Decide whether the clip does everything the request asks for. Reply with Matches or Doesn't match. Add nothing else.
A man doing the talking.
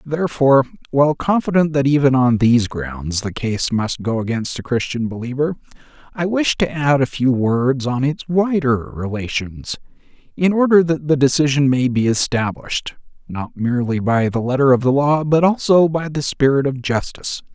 Matches